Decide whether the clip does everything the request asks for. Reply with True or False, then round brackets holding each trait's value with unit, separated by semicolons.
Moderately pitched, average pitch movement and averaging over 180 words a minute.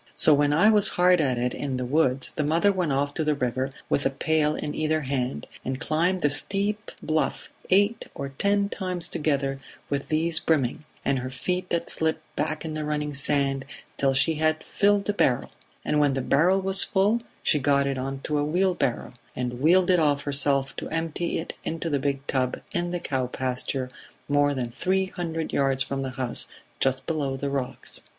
True (150 Hz; 3.9 semitones; 195 wpm)